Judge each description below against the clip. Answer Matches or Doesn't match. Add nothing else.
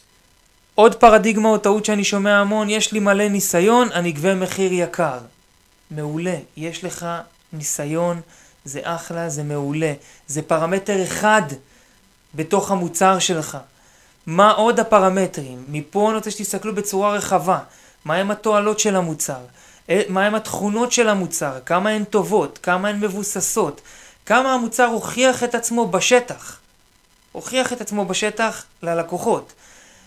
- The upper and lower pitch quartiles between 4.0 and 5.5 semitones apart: Matches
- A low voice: Doesn't match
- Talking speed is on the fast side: Doesn't match